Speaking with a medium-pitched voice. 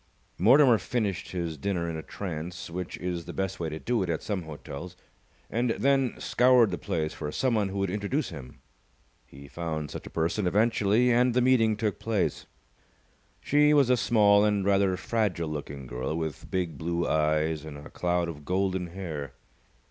No: very low, 90 Hz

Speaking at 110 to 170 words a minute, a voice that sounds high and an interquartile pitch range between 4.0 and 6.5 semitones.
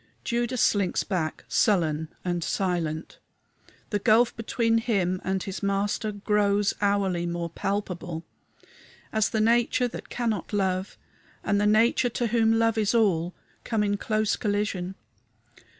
No: slow, 135 wpm; high, 205 Hz; average, 3.4 semitones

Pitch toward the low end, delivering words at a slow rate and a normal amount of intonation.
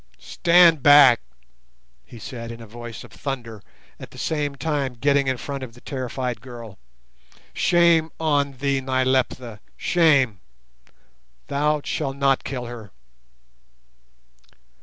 Yes: low, 130 Hz; slow, 115 wpm; average, 3.4 semitones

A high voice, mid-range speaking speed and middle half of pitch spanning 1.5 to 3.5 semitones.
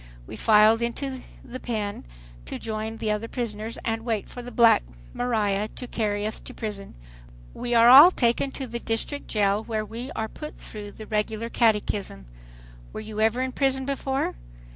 Yes: high, 225 Hz; average, 175 wpm; narrow, 2.5 semitones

